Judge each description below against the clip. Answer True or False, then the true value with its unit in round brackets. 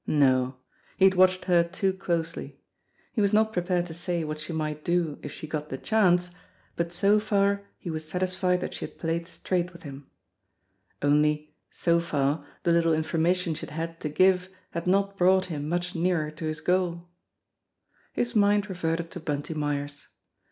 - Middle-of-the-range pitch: True (170 Hz)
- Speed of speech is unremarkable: True (180 wpm)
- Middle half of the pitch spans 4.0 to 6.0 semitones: False (3.0 semitones)